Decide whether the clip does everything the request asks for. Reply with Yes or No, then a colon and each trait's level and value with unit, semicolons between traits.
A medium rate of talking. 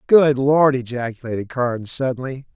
No: slow, 120 wpm